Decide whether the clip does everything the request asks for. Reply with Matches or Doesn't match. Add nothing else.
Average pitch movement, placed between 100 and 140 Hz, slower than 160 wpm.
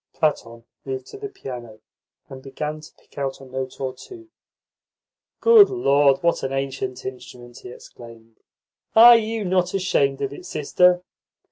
Doesn't match